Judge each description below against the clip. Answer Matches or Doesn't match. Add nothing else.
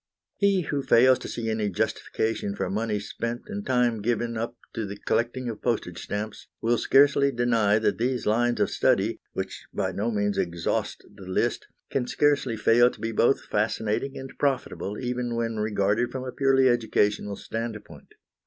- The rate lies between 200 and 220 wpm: Doesn't match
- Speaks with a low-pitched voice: Matches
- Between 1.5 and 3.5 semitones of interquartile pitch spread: Matches